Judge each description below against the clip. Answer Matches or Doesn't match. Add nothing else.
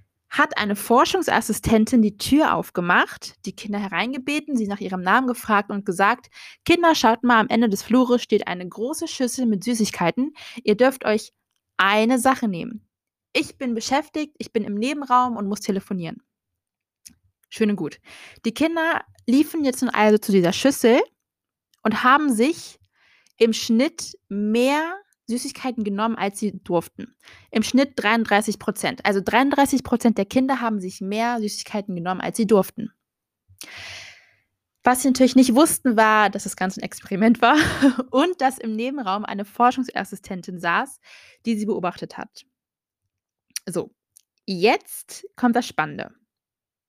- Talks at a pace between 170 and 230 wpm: Doesn't match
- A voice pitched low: Doesn't match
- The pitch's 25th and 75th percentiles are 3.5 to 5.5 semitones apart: Matches